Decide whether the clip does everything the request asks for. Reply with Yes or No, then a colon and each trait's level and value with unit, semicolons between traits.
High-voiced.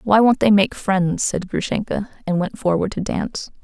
Yes: high, 200 Hz